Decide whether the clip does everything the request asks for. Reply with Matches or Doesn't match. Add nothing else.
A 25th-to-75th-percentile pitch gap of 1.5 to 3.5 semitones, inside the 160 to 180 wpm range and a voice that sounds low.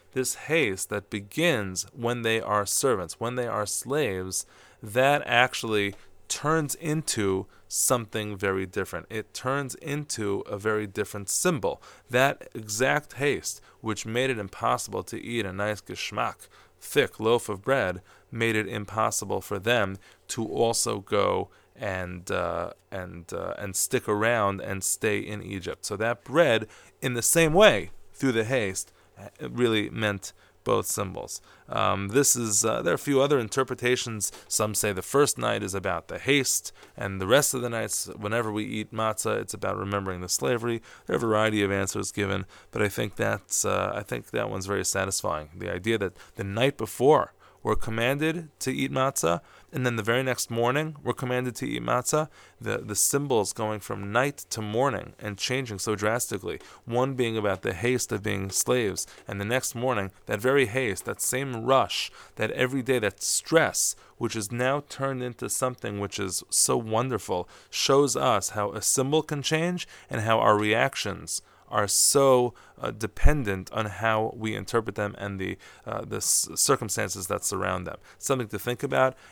Doesn't match